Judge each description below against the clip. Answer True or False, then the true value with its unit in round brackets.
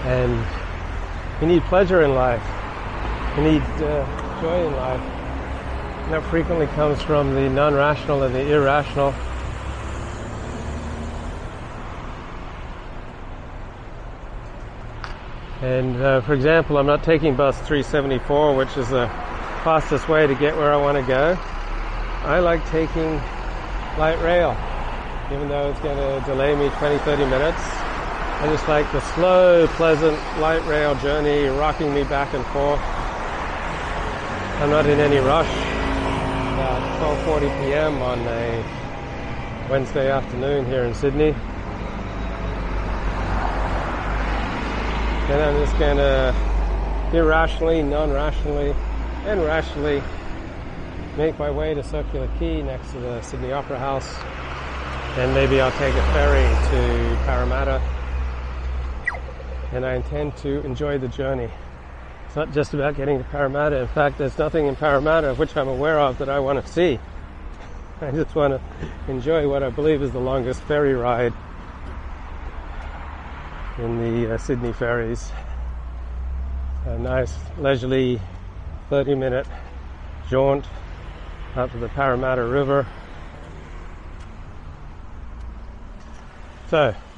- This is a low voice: True (130 Hz)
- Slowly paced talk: True (120 wpm)